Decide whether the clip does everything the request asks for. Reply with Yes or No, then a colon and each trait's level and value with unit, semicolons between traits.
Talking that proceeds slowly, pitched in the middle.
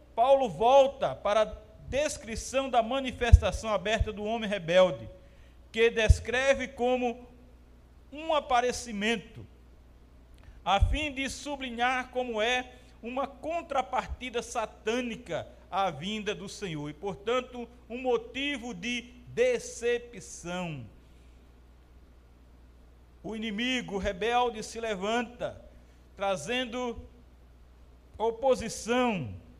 No: slow, 85 wpm; high, 225 Hz